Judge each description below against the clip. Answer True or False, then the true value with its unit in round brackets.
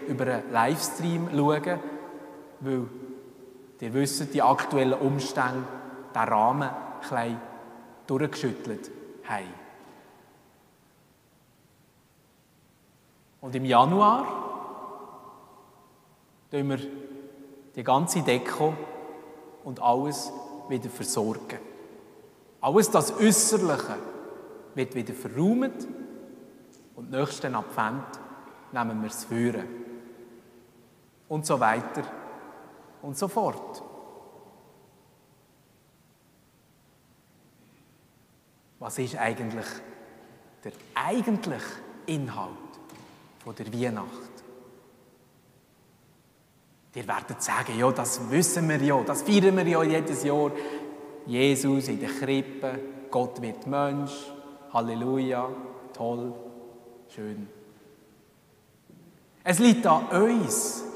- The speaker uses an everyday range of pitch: True (4.0 semitones)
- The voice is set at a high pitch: False (135 Hz)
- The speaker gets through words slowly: True (80 wpm)